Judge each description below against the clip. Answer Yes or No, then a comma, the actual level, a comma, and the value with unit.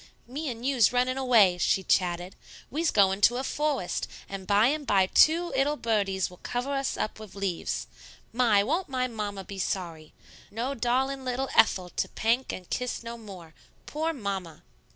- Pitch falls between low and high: No, high, 230 Hz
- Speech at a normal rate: Yes, average, 175 wpm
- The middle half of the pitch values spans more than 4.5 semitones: Yes, wide, 5.5 semitones